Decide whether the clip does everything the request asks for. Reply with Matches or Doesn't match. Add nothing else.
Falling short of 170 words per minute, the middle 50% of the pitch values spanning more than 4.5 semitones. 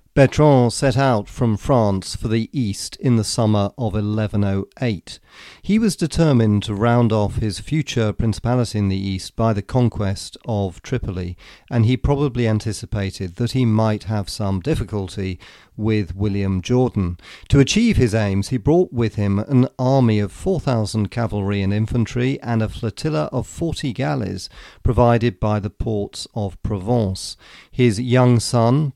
Doesn't match